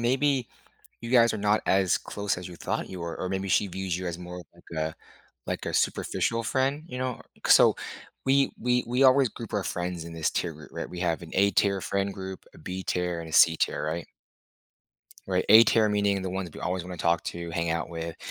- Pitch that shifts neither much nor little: Yes, average, 4.6 semitones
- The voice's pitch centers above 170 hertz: No, very low, 95 Hz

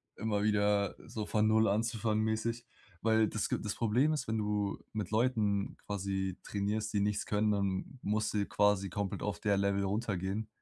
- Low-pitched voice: Yes, low, 105 Hz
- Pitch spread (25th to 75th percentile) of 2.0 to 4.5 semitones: No, narrow, 1.6 semitones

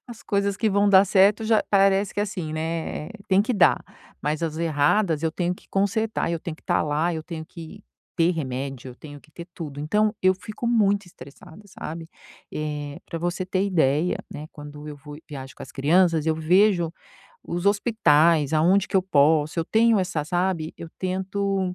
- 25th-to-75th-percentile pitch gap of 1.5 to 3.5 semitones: No, average, 4.3 semitones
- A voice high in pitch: No, medium, 170 Hz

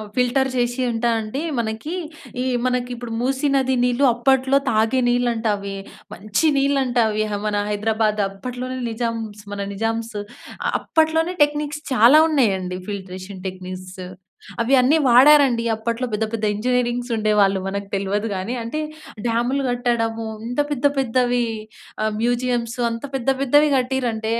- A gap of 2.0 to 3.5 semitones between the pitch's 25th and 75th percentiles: Yes, average, 3.2 semitones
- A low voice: No, high, 235 Hz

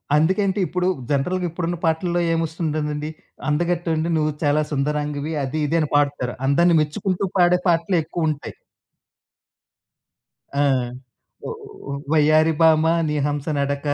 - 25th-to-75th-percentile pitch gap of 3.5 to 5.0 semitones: No, average, 2.7 semitones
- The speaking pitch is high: No, medium, 155 Hz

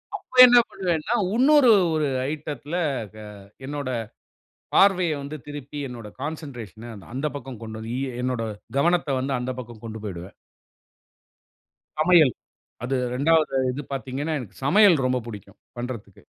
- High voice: No, medium, 140 Hz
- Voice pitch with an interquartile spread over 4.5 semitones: Yes, average, 4.9 semitones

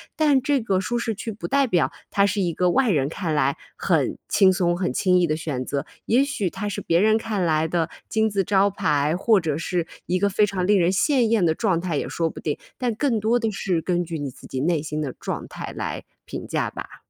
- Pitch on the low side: No, medium, 185 Hz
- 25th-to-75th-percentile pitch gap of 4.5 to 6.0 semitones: Yes, average, 4.9 semitones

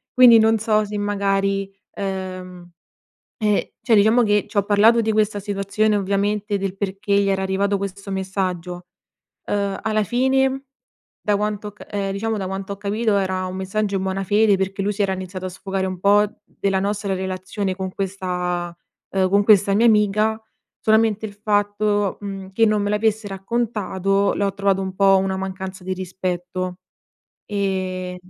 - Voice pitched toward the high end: Yes, high, 200 Hz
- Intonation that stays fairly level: Yes, narrow, 1.7 semitones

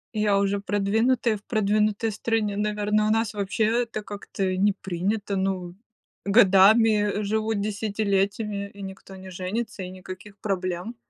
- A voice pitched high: Yes, high, 205 Hz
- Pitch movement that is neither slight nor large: No, narrow, 1.8 semitones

